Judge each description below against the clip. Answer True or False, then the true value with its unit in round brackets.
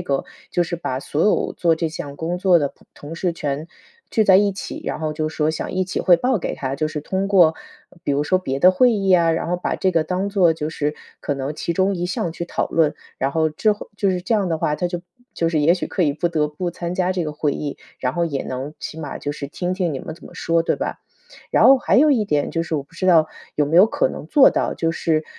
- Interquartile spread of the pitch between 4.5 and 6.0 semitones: False (3.4 semitones)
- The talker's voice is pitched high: False (165 Hz)